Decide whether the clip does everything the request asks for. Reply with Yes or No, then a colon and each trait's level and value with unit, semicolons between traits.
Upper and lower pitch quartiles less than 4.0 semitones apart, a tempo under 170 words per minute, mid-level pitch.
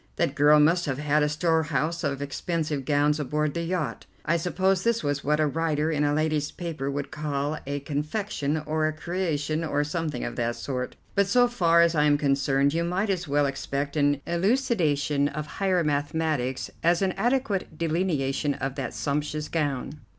No: average, 2.8 semitones; average, 180 wpm; medium, 150 Hz